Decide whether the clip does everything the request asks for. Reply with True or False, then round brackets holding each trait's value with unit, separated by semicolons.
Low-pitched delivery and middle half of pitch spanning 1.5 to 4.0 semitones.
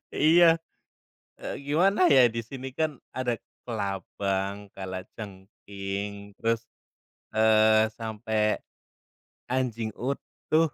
False (110 Hz; 4.5 semitones)